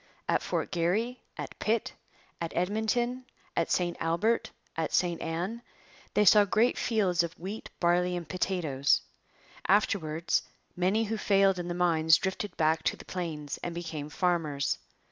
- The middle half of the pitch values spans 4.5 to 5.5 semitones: No, average, 3.8 semitones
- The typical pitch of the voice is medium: Yes, medium, 180 Hz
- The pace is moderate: Yes, average, 145 wpm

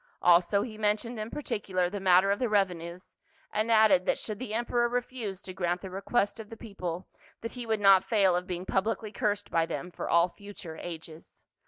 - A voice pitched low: No, high, 200 Hz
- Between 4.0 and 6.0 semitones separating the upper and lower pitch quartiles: No, average, 3.4 semitones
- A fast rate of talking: Yes, fast, 210 wpm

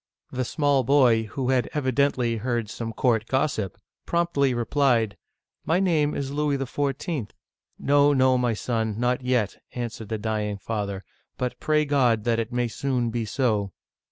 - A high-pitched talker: No, low, 125 Hz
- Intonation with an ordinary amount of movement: Yes, average, 3.7 semitones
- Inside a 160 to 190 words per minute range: Yes, average, 170 wpm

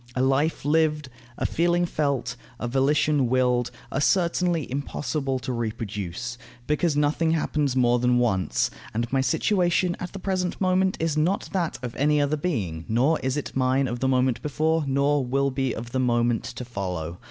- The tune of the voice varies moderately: Yes, average, 4.2 semitones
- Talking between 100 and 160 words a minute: No, average, 175 wpm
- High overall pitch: No, low, 135 Hz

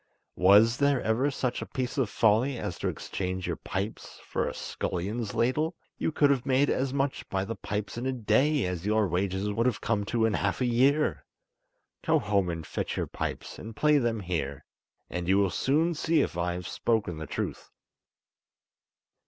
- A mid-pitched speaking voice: No, low, 110 Hz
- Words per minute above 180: Yes, average, 190 wpm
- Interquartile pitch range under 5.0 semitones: No, wide, 5.5 semitones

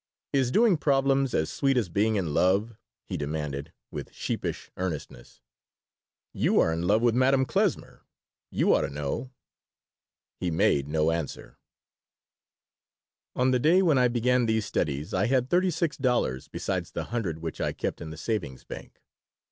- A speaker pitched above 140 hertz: No, low, 110 Hz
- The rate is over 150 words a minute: Yes, average, 160 wpm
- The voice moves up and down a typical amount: No, wide, 8.3 semitones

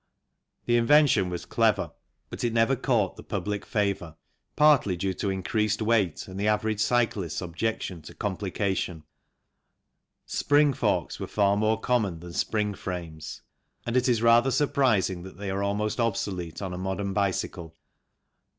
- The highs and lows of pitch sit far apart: No, average, 3.8 semitones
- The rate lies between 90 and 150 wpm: No, average, 160 wpm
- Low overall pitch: Yes, low, 100 Hz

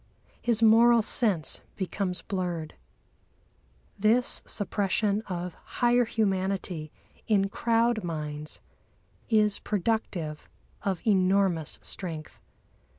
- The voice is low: No, high, 195 Hz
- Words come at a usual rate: No, slow, 85 wpm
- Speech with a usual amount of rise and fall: Yes, average, 4.2 semitones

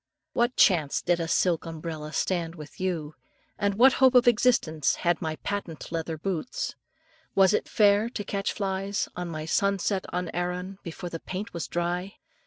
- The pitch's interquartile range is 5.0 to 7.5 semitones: No, average, 3.4 semitones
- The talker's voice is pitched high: No, medium, 180 Hz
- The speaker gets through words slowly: No, average, 165 wpm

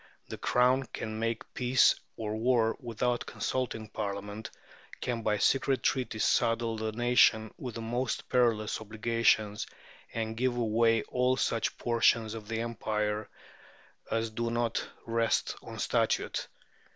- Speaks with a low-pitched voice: Yes, low, 115 Hz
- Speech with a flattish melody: Yes, narrow, 1.8 semitones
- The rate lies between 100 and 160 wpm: Yes, slow, 135 wpm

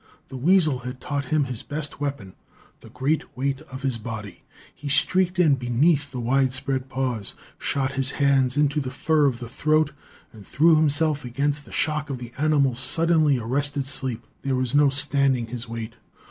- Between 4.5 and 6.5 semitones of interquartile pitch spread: No, average, 2.8 semitones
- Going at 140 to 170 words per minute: No, average, 180 wpm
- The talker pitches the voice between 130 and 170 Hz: Yes, low, 135 Hz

